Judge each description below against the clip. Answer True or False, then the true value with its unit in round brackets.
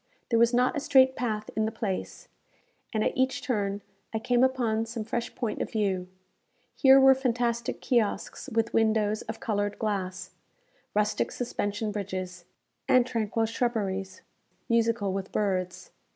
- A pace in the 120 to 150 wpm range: True (145 wpm)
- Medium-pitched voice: False (220 Hz)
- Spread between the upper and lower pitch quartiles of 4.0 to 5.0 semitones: False (2.8 semitones)